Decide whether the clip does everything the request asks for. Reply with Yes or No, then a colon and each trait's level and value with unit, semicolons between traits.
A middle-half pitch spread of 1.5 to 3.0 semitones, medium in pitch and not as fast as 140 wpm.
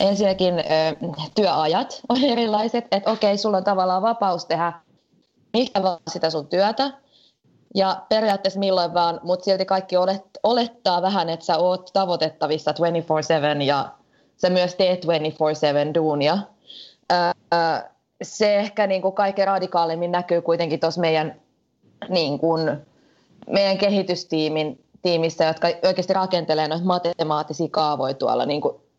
No: average, 3.4 semitones; medium, 180 Hz; average, 120 wpm